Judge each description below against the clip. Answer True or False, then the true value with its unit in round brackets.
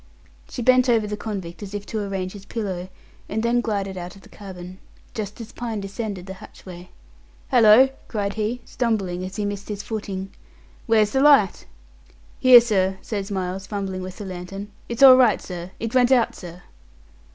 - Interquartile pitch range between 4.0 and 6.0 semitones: False (3.2 semitones)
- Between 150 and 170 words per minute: False (180 wpm)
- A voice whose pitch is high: True (205 Hz)